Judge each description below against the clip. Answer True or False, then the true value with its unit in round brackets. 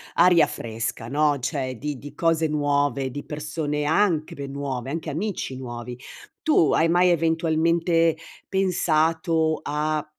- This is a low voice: False (155 Hz)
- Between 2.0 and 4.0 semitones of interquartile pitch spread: True (2.6 semitones)